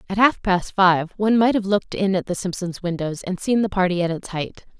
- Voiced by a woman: Yes, female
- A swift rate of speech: Yes, fast, 250 wpm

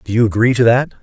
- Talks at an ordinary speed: No, fast, 290 wpm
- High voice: No, low, 115 Hz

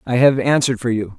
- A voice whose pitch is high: No, low, 125 Hz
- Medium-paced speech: No, fast, 255 wpm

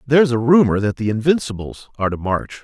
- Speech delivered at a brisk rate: Yes, fast, 225 wpm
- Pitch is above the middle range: No, low, 120 Hz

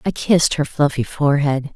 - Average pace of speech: Yes, average, 170 wpm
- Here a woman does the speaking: Yes, female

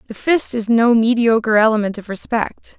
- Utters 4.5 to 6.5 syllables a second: Yes, 5.0 syllables/s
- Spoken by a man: No, female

